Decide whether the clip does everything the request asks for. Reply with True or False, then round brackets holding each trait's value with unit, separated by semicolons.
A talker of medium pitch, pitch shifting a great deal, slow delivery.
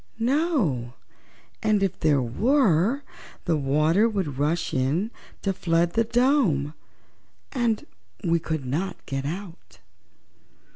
True (175 Hz; 7.4 semitones; 110 wpm)